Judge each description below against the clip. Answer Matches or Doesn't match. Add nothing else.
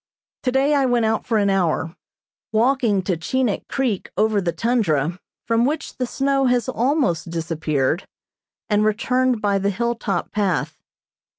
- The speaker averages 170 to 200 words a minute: Doesn't match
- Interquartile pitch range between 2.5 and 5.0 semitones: Doesn't match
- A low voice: Doesn't match